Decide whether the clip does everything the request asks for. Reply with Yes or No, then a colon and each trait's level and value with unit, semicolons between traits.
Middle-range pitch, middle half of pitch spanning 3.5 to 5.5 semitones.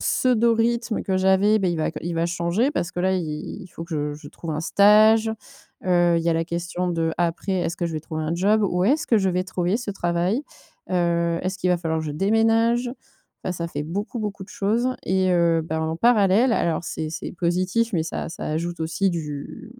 Yes: medium, 180 Hz; average, 3.9 semitones